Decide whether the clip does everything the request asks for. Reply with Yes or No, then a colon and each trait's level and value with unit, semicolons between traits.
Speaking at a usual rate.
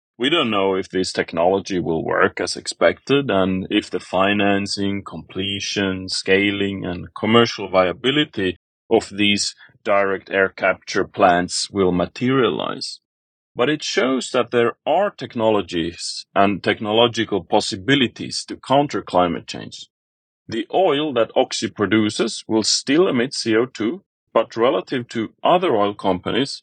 No: slow, 125 wpm